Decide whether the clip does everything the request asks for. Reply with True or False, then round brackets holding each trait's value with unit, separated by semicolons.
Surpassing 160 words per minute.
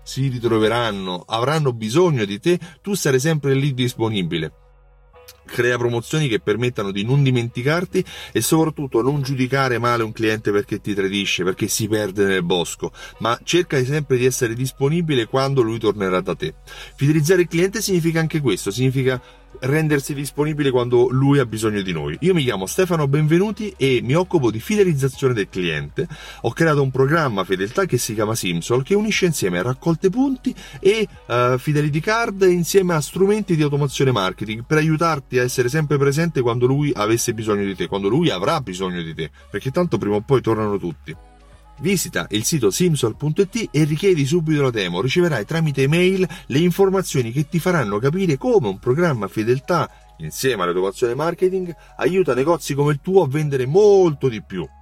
True (170 wpm)